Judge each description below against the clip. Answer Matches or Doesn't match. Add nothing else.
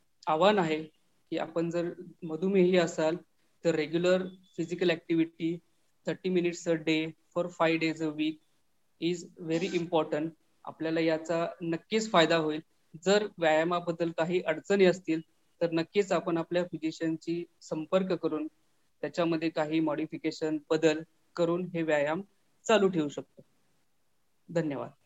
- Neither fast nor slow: Doesn't match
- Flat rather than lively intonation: Matches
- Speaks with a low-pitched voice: Doesn't match